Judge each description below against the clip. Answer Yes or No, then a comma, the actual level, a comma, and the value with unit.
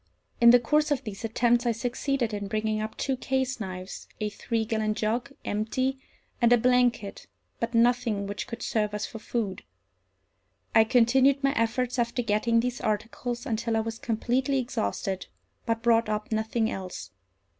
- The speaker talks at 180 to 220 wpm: No, average, 165 wpm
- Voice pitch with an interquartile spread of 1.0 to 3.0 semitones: Yes, narrow, 2.4 semitones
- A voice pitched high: Yes, high, 230 Hz